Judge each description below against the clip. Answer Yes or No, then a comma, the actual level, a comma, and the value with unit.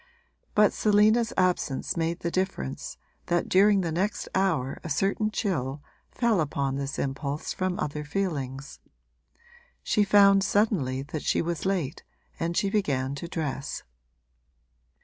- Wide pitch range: Yes, wide, 5.9 semitones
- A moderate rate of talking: No, slow, 130 wpm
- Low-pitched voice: No, medium, 170 Hz